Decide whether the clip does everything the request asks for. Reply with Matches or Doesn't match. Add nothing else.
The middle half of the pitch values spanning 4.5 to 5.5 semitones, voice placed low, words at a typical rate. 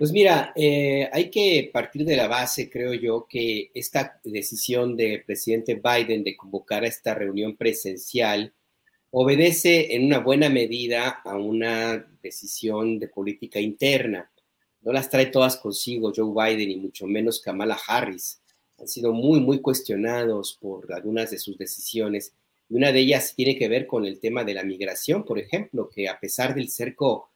Doesn't match